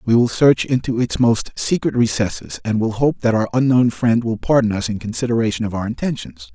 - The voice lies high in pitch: No, low, 115 Hz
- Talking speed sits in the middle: No, fast, 210 wpm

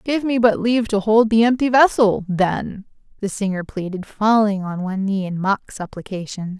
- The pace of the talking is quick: No, average, 180 wpm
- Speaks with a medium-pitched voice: No, high, 210 Hz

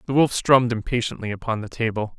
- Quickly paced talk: No, average, 190 wpm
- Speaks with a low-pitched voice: Yes, low, 115 Hz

